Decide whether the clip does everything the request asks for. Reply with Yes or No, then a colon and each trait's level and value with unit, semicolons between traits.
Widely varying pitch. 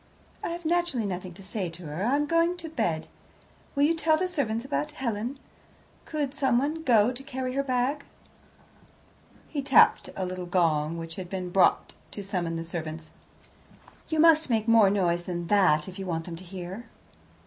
Yes: wide, 8.1 semitones